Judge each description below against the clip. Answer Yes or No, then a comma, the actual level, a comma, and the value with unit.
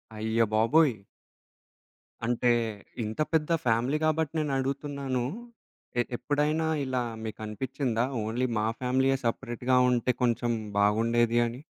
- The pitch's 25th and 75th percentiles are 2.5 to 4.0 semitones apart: Yes, average, 3.1 semitones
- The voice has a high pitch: No, low, 125 Hz